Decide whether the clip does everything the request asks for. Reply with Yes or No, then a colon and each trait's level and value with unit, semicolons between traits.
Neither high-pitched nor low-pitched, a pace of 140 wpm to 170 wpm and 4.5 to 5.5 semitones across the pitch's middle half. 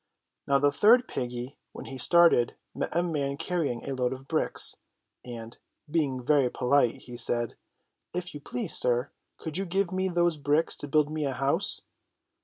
No: medium, 145 Hz; average, 180 wpm; average, 5.2 semitones